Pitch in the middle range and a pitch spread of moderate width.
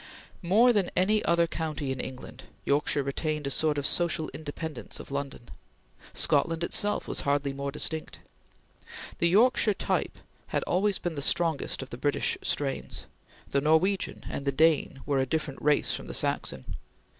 Yes: medium, 155 Hz; average, 3.6 semitones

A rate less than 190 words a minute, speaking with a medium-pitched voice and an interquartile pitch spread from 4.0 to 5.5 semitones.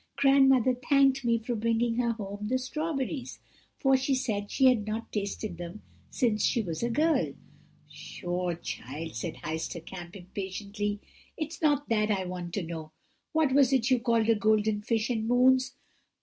No: average, 170 wpm; high, 225 Hz; average, 4.5 semitones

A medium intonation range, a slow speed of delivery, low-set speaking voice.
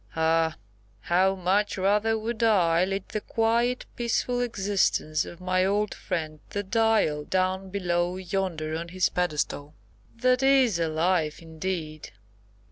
No: average, 4.3 semitones; slow, 130 wpm; medium, 185 Hz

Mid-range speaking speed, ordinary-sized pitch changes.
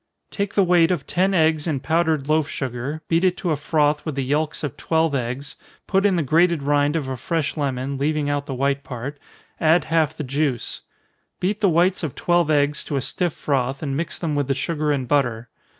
No: fast, 220 wpm; average, 3.1 semitones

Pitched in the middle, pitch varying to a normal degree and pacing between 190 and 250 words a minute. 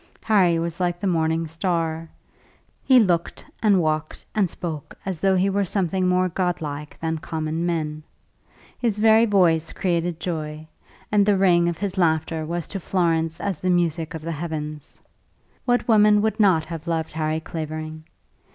No: medium, 170 Hz; average, 3.1 semitones; average, 160 wpm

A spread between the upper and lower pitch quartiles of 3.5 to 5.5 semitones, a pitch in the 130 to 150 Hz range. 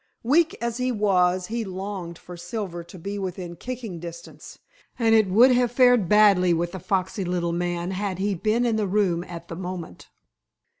No: average, 4.0 semitones; high, 190 Hz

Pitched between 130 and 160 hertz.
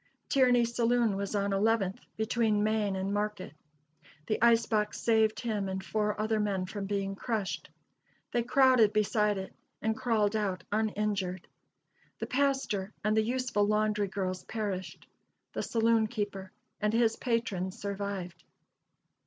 No: high, 210 Hz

